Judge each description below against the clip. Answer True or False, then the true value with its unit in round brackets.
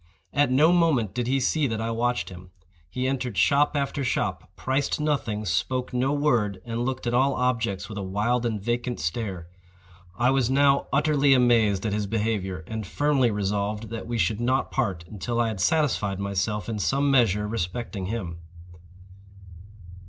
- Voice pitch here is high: False (115 Hz)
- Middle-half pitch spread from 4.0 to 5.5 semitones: True (4.3 semitones)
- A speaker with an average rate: True (170 wpm)